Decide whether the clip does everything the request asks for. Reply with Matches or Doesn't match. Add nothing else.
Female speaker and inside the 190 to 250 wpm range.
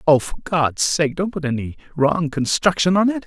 Doesn't match